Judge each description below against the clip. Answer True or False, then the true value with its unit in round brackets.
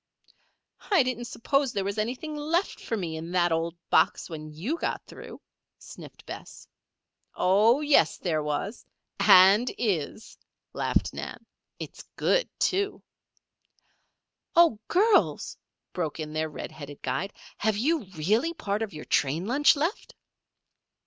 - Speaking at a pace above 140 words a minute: False (135 wpm)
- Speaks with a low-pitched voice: False (210 Hz)